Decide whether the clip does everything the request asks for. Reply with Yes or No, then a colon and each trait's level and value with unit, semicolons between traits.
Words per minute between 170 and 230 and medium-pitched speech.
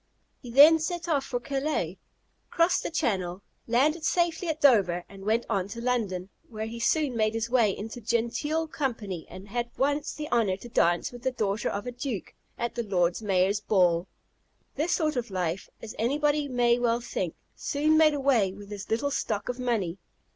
No: average, 185 wpm; high, 235 Hz